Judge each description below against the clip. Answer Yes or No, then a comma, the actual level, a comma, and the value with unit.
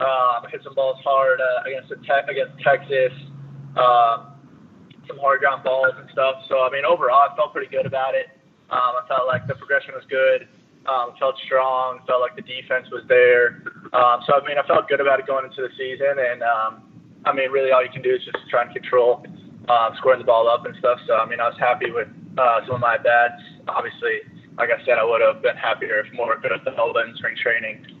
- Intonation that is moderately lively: No, wide, 6.3 semitones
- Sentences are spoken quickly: Yes, fast, 235 wpm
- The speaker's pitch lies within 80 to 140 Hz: Yes, low, 135 Hz